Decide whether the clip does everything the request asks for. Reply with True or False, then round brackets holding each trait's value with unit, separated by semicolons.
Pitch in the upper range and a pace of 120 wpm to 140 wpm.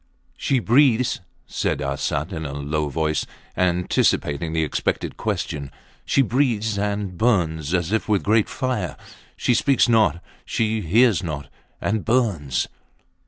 False (100 Hz; 135 wpm)